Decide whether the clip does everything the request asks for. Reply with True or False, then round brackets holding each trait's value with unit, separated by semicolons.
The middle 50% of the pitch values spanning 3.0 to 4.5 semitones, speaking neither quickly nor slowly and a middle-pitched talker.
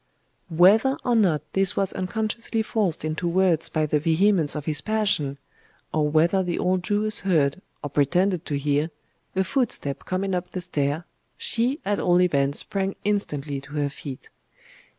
False (4.9 semitones; 160 wpm; 180 Hz)